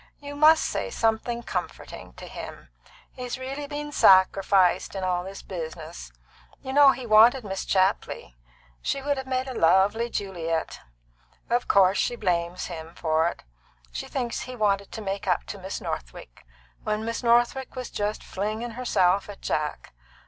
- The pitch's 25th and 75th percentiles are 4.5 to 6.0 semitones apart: Yes, average, 5.2 semitones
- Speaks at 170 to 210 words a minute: No, average, 155 wpm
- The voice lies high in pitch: Yes, high, 210 Hz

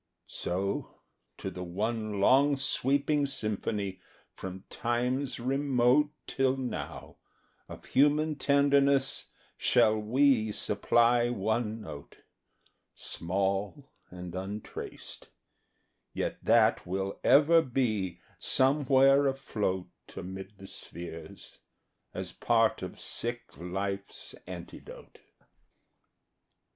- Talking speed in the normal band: No, slow, 85 wpm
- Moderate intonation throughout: No, wide, 5.8 semitones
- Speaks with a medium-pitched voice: No, low, 115 Hz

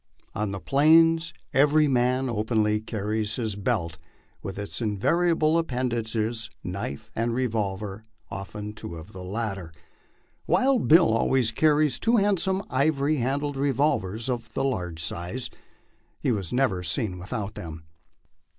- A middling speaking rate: No, slow, 130 wpm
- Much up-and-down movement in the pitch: Yes, wide, 5.8 semitones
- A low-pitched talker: Yes, low, 115 Hz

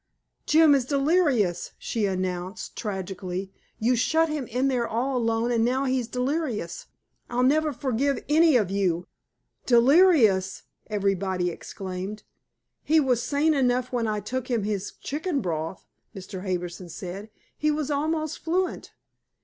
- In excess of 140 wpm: No, slow, 135 wpm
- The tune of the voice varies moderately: No, wide, 6.6 semitones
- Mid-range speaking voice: No, high, 240 Hz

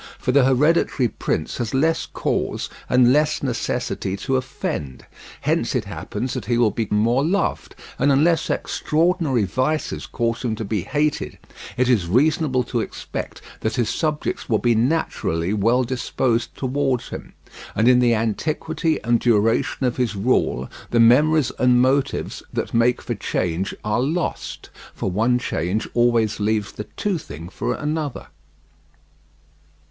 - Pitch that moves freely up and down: No, average, 4.2 semitones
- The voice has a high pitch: No, low, 125 Hz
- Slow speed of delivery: No, average, 145 wpm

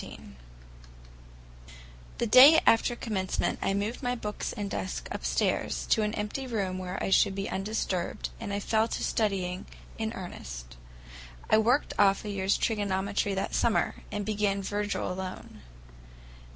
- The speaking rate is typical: Yes, average, 145 wpm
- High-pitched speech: Yes, high, 205 Hz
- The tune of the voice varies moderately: No, narrow, 2.3 semitones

